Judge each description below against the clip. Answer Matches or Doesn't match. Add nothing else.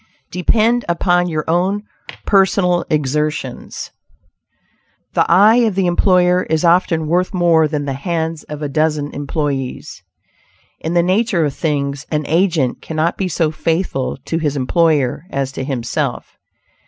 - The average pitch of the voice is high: Doesn't match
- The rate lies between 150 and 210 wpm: Doesn't match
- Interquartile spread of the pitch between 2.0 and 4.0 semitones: Matches